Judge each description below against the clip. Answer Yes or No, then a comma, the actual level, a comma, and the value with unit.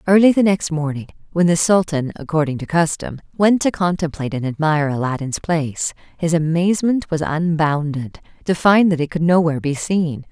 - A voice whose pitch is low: No, medium, 165 Hz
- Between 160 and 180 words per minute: Yes, average, 170 wpm